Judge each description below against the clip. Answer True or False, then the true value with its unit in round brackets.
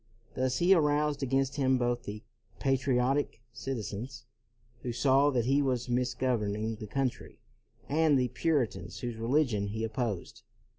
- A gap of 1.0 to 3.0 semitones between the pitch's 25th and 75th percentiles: True (2.7 semitones)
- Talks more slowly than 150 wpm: True (140 wpm)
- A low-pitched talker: True (125 Hz)